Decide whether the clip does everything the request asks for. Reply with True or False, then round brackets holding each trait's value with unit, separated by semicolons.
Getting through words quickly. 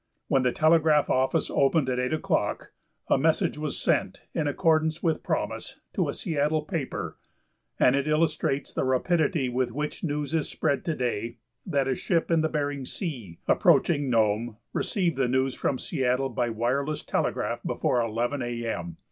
False (165 wpm)